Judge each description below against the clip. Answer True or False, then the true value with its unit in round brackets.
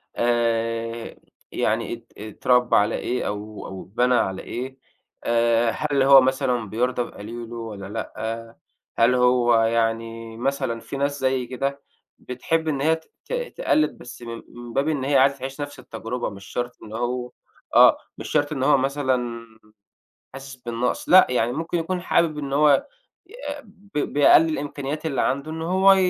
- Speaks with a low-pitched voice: True (125 Hz)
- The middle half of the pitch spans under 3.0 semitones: False (3.5 semitones)